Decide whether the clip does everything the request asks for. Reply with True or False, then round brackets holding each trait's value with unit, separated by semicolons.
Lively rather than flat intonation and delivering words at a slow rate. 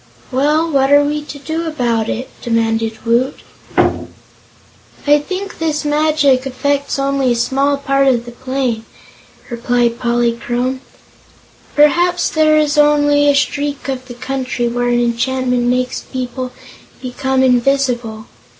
False (3.1 semitones; 130 wpm)